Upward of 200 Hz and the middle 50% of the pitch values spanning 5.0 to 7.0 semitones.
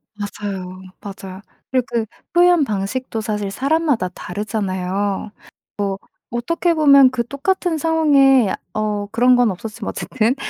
Yes: high, 230 Hz; wide, 5.4 semitones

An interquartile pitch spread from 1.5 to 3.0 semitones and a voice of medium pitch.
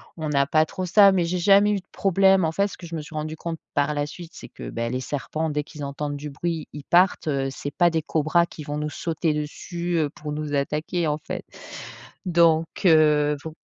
Yes: narrow, 2.6 semitones; medium, 155 Hz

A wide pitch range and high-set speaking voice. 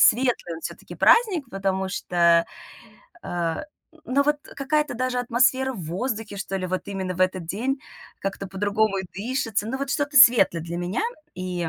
Yes: wide, 6.0 semitones; high, 205 Hz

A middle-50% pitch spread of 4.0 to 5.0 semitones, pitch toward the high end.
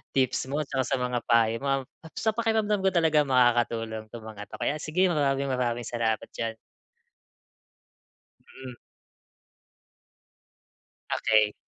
No: average, 4.6 semitones; low, 130 Hz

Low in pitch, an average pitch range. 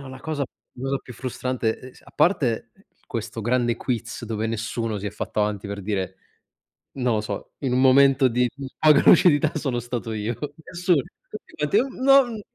Yes: low, 125 Hz; average, 4.1 semitones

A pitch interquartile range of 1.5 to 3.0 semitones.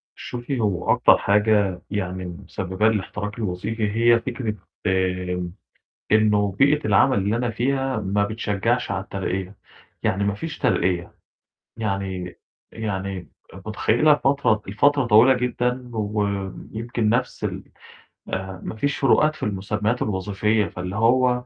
No: average, 3.9 semitones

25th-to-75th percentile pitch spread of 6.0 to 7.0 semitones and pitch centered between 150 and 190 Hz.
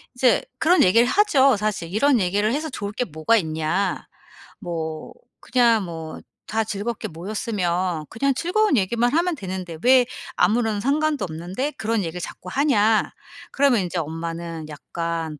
No: wide, 6.6 semitones; high, 205 Hz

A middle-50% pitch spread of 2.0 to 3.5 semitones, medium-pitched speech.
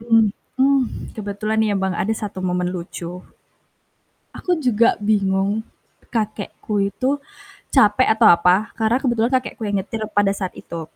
No: average, 2.8 semitones; high, 210 Hz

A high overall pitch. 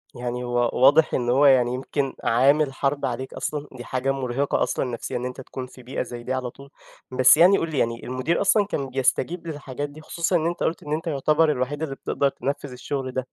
No: low, 135 Hz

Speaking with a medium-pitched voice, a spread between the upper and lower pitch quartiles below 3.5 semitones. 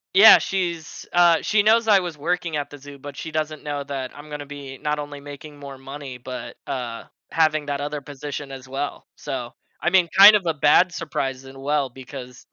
Yes: medium, 145 Hz; average, 3.1 semitones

